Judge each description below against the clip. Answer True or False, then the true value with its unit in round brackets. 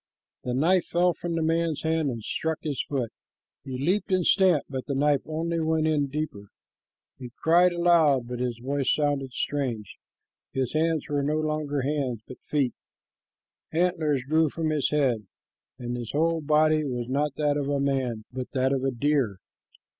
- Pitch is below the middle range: False (145 Hz)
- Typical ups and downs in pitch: True (3.5 semitones)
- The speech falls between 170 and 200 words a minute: True (175 wpm)